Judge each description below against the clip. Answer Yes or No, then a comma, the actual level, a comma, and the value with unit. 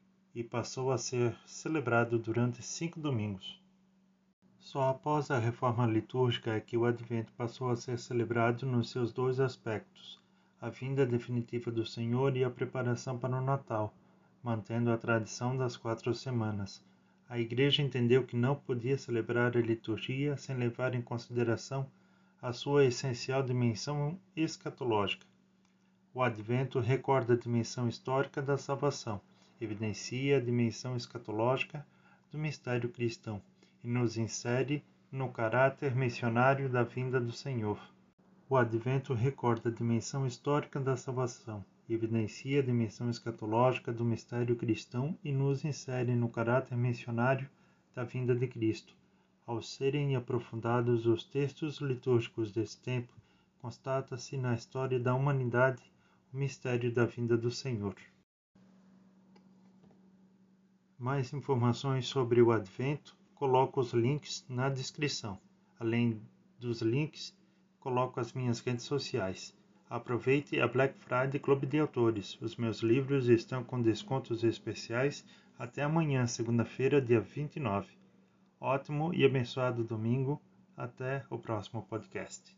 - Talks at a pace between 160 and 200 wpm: No, average, 125 wpm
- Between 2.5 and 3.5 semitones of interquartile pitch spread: Yes, average, 2.8 semitones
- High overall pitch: No, low, 125 Hz